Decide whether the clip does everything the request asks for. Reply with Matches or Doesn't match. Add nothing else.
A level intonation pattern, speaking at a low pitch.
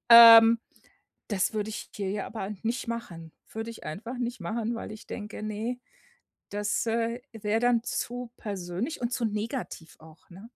Doesn't match